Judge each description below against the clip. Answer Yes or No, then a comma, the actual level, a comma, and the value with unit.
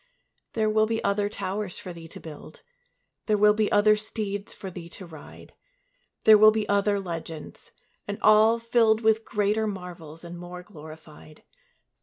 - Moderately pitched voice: No, high, 205 Hz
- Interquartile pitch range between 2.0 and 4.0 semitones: Yes, average, 3.7 semitones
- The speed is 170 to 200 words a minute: No, average, 160 wpm